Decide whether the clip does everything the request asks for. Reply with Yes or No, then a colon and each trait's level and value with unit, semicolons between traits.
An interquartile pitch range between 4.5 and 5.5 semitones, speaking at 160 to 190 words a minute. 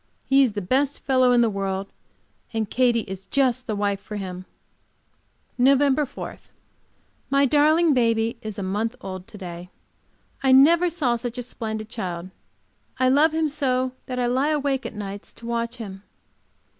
Yes: average, 4.9 semitones; average, 165 wpm